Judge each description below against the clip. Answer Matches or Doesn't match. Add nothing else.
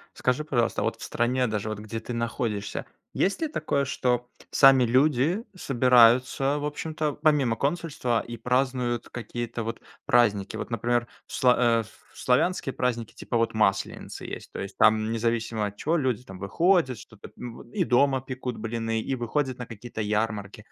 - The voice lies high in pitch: Doesn't match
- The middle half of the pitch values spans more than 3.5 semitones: Doesn't match